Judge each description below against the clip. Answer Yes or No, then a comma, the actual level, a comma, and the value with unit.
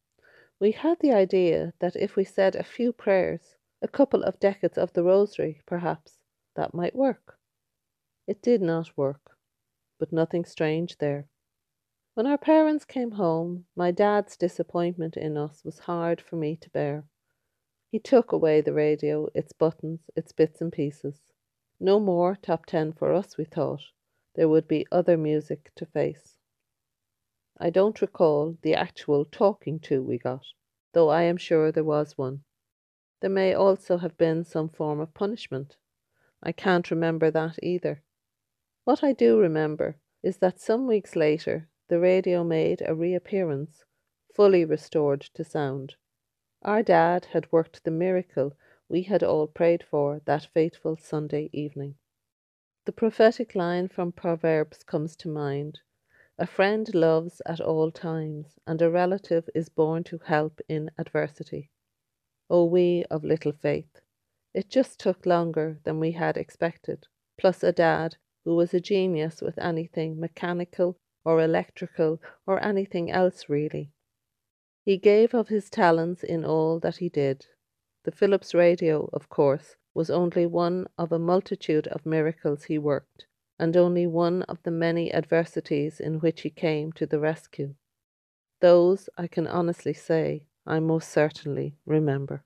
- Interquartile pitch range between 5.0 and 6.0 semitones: No, average, 3.0 semitones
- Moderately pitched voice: Yes, medium, 165 Hz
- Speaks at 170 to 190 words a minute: No, average, 155 wpm